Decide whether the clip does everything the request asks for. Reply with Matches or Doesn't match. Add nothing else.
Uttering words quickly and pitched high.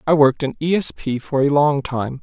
Doesn't match